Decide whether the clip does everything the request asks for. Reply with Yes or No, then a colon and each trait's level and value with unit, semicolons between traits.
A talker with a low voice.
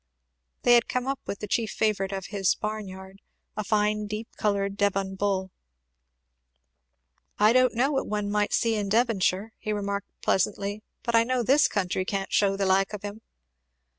No: high, 205 Hz